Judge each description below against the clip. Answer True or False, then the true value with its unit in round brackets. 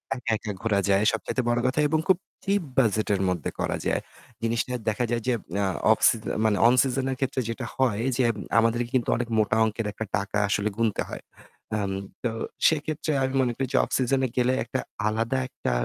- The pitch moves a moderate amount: True (3.4 semitones)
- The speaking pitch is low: True (120 Hz)